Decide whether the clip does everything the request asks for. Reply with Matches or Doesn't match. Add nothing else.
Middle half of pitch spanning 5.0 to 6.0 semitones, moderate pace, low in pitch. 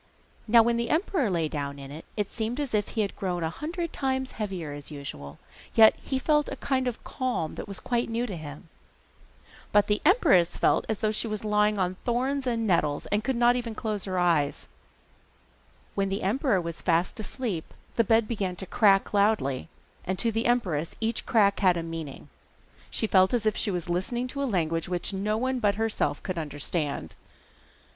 Doesn't match